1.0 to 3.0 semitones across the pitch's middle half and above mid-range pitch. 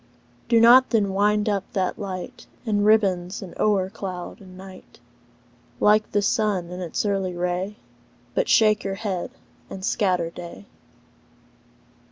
Yes: narrow, 2.4 semitones; high, 195 Hz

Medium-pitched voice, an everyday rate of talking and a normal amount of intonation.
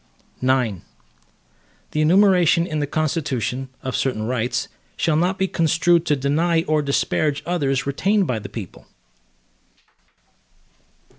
No: medium, 150 Hz; slow, 120 wpm; average, 4.3 semitones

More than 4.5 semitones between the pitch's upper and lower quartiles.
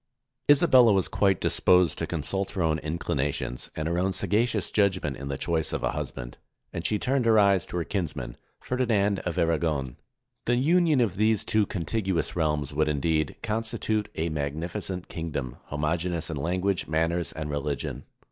Yes: average, 5.1 semitones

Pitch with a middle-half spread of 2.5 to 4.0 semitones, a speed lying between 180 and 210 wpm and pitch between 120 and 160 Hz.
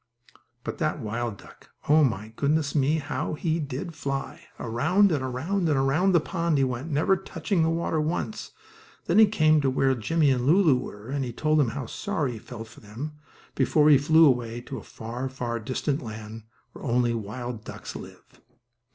No: average, 4.8 semitones; average, 190 wpm; medium, 140 Hz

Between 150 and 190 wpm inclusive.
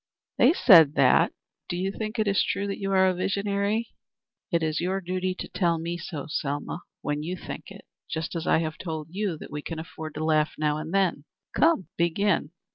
No: average, 200 wpm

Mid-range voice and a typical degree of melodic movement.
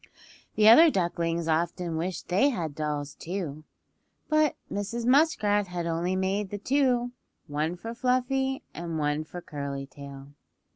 No: medium, 180 Hz; wide, 7.0 semitones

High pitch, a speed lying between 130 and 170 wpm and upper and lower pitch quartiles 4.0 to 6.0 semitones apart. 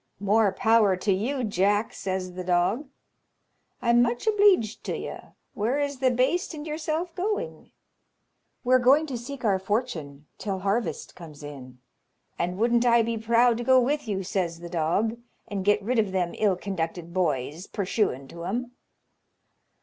Yes: high, 215 Hz; average, 160 wpm; average, 5.3 semitones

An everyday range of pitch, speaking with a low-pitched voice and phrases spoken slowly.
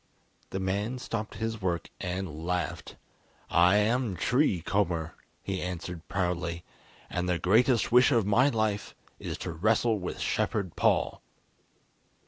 Yes: average, 3.9 semitones; very low, 95 Hz; slow, 130 wpm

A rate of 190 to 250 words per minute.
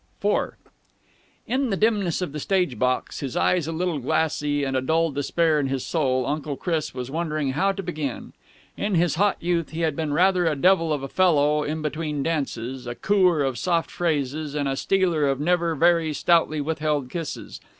Yes: average, 195 wpm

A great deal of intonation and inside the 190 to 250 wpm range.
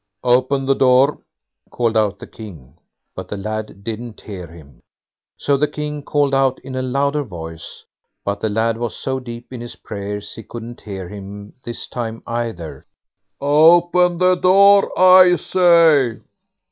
No: wide, 5.8 semitones; average, 155 wpm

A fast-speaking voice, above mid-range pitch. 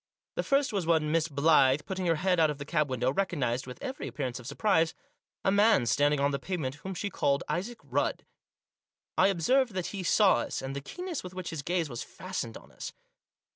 No: fast, 215 wpm; medium, 165 Hz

